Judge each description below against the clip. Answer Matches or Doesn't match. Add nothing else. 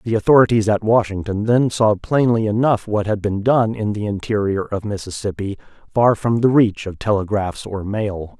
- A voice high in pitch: Doesn't match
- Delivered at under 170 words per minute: Doesn't match